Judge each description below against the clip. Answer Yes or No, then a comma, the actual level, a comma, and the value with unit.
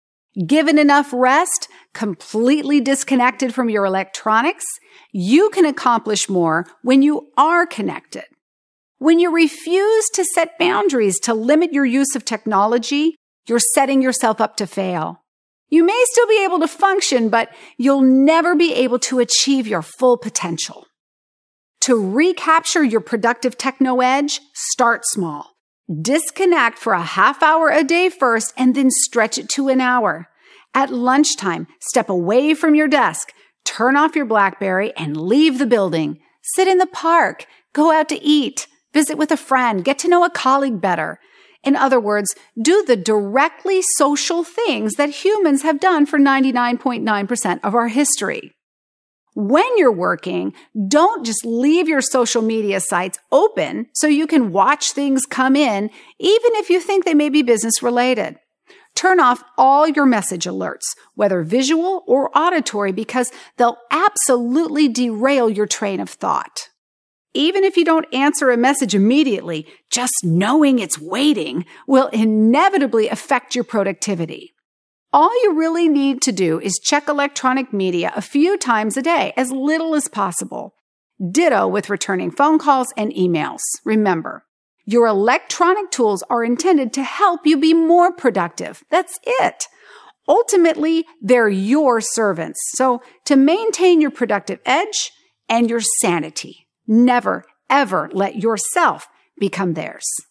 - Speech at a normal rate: Yes, average, 145 wpm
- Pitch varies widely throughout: Yes, wide, 6.2 semitones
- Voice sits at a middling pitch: No, very high, 265 Hz